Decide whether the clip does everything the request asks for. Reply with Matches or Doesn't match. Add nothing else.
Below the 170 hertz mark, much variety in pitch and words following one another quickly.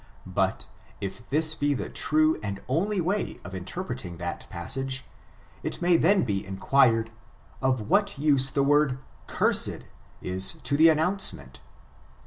Doesn't match